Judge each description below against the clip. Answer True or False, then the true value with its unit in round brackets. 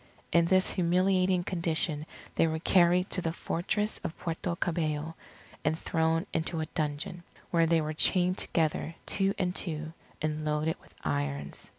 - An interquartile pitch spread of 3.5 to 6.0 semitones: False (2.4 semitones)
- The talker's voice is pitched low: False (165 Hz)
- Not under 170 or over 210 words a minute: False (155 wpm)